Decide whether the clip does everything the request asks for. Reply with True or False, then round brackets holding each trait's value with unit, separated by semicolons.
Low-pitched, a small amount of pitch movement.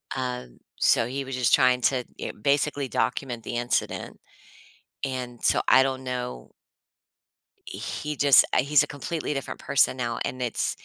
True (130 Hz; 2.1 semitones)